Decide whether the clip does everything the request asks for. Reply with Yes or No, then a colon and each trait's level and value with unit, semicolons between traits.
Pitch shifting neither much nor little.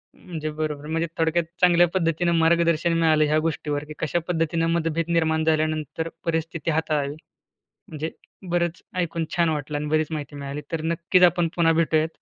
No: narrow, 1.5 semitones